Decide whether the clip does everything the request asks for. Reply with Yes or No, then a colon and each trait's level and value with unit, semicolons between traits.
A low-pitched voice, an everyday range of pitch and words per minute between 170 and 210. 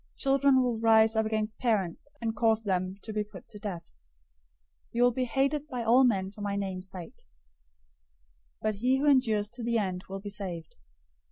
No: high, 220 Hz; average, 3.6 semitones; average, 190 wpm